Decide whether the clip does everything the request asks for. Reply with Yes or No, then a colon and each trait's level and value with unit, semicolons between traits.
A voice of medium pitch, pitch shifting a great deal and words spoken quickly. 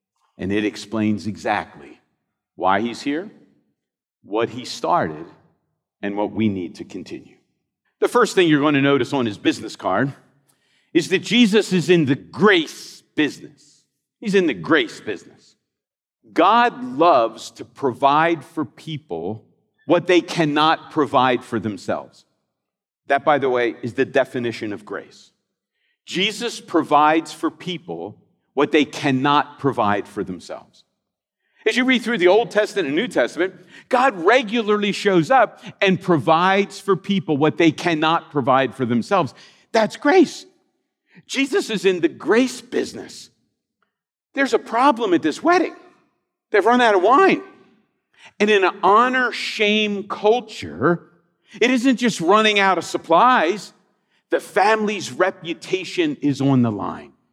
No: medium, 180 Hz; wide, 8.8 semitones; average, 140 wpm